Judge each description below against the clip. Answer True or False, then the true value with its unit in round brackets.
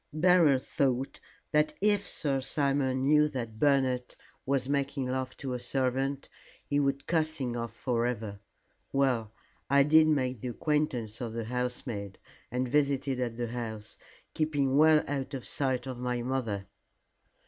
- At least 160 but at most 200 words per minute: False (150 wpm)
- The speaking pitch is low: True (130 Hz)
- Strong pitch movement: False (2.6 semitones)